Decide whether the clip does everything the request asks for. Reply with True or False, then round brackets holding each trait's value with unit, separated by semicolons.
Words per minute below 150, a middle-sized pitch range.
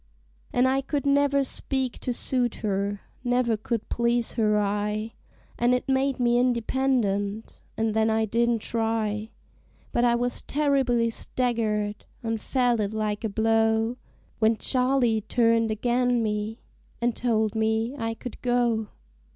False (140 wpm; 2.1 semitones)